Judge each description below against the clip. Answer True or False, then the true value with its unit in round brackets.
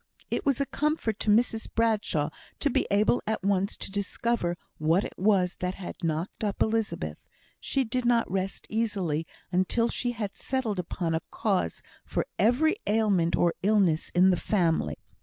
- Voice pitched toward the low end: False (200 Hz)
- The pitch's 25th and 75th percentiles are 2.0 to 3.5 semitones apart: False (4.2 semitones)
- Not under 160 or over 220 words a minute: True (165 wpm)